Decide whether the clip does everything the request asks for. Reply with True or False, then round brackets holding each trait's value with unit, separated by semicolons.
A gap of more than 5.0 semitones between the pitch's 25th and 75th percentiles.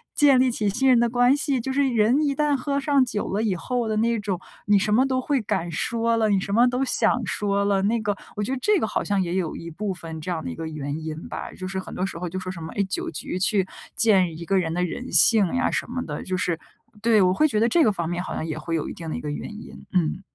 True (5.6 semitones)